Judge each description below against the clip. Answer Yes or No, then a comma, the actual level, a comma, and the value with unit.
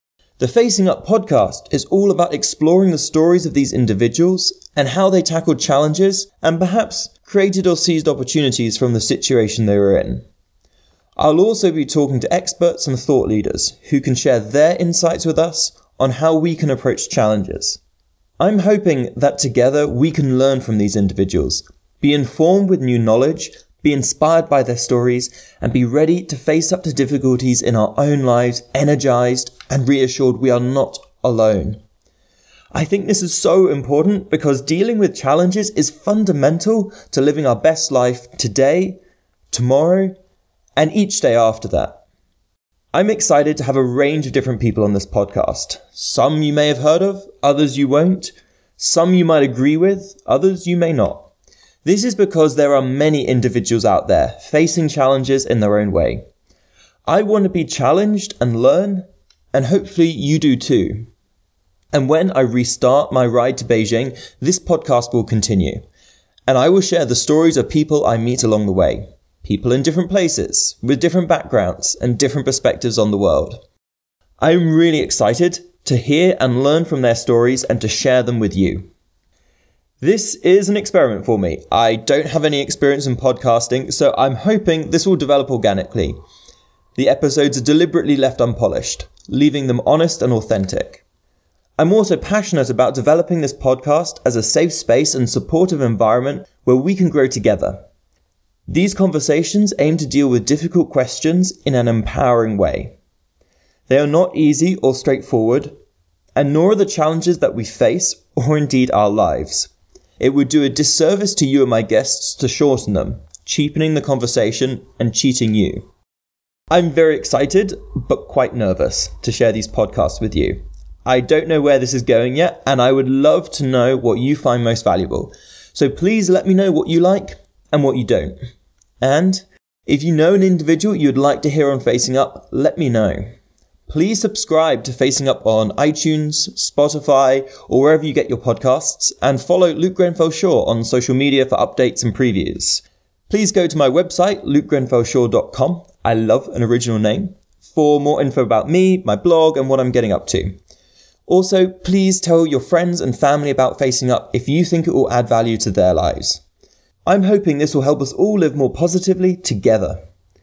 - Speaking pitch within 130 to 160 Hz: Yes, medium, 140 Hz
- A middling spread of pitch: No, wide, 5.7 semitones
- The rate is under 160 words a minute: No, average, 175 wpm